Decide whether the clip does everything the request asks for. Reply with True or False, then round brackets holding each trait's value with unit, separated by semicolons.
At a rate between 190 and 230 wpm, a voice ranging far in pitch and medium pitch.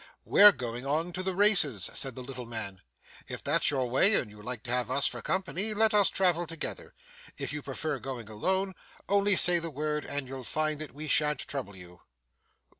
True (200 wpm; 6.5 semitones; 150 Hz)